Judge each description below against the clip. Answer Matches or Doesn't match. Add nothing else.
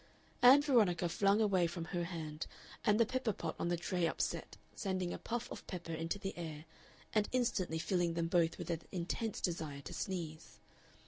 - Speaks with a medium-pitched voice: Matches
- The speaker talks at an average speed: Matches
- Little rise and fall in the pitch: Doesn't match